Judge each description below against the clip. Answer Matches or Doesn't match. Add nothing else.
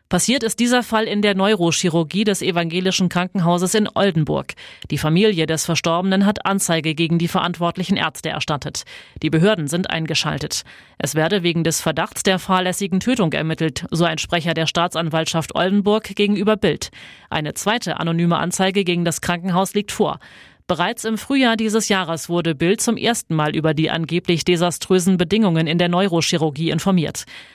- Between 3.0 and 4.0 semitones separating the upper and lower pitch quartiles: Matches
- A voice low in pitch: Doesn't match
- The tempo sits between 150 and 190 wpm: Matches